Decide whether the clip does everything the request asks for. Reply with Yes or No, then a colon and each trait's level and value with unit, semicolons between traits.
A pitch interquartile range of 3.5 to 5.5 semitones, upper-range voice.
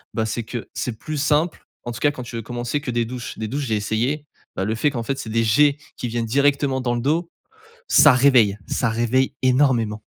No: average, 3.8 semitones; low, 125 Hz